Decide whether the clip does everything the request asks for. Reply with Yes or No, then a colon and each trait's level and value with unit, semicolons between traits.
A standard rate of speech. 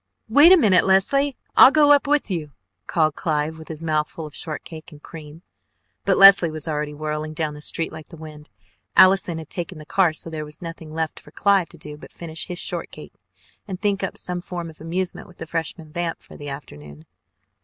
No: fast, 210 wpm